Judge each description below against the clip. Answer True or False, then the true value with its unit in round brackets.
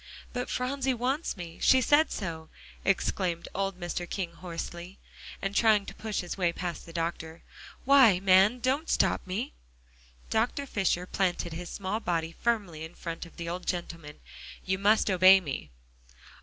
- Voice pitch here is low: False (185 Hz)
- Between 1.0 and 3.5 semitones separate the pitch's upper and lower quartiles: False (4.4 semitones)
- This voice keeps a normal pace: True (155 wpm)